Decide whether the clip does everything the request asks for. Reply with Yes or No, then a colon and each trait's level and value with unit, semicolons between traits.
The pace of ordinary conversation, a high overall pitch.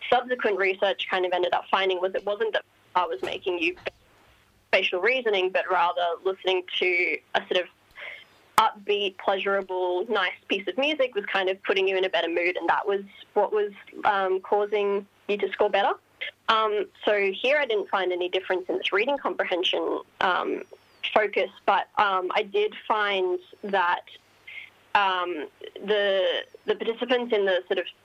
Yes: average, 165 wpm; high, 205 Hz